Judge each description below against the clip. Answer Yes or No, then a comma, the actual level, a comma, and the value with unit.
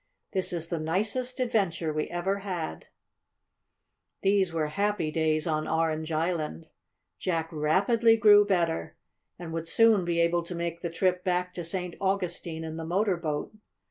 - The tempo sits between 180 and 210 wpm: No, average, 155 wpm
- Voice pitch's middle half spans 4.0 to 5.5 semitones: No, average, 3.2 semitones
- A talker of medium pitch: Yes, medium, 170 Hz